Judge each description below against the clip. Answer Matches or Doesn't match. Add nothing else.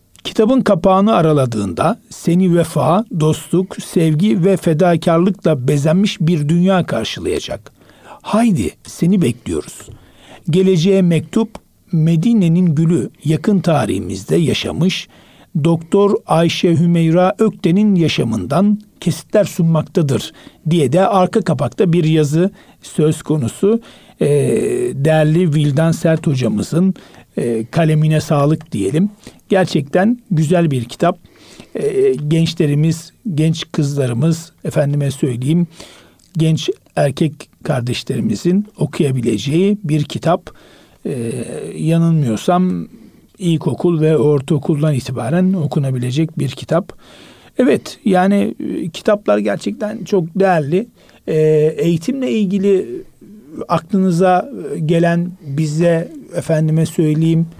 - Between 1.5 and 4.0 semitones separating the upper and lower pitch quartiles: Matches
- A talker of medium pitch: Matches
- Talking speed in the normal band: Doesn't match